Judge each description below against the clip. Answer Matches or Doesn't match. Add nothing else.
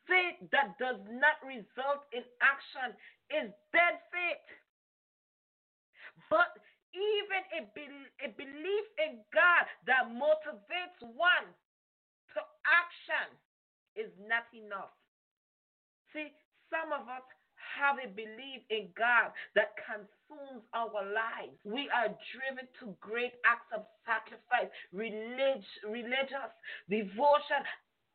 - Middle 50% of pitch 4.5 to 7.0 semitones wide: Matches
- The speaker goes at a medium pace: Doesn't match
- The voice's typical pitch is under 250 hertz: Doesn't match